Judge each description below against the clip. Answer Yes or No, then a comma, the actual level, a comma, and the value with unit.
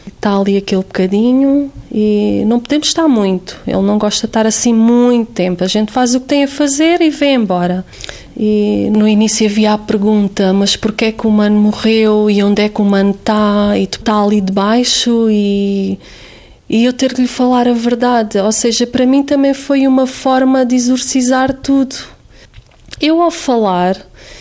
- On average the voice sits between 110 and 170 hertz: No, high, 225 Hz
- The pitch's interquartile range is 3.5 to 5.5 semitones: Yes, average, 3.8 semitones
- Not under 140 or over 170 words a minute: No, fast, 185 wpm